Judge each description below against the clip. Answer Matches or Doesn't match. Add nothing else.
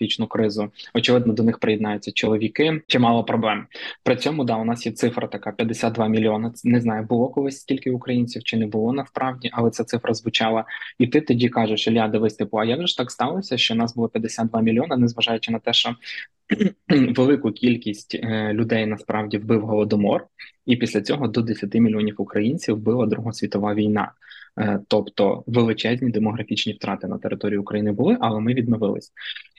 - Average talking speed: Doesn't match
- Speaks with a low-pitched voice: Matches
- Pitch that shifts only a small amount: Matches